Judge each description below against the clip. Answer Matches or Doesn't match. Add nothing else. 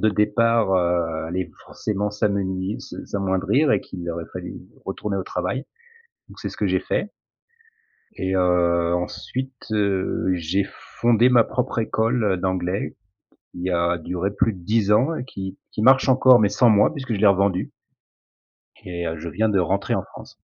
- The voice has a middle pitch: Doesn't match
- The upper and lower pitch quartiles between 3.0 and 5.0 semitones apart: Matches